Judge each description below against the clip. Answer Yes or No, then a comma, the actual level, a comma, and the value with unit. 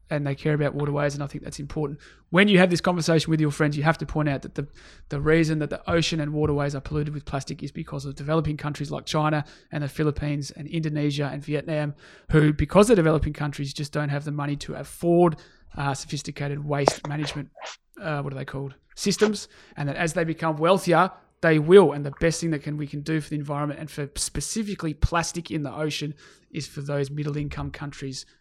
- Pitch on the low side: No, medium, 150 Hz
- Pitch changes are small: Yes, narrow, 1.8 semitones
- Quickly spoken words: Yes, fast, 220 wpm